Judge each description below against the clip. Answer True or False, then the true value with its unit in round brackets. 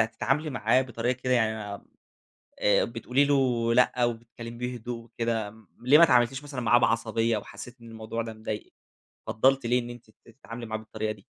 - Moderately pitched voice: False (115 Hz)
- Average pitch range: False (2.0 semitones)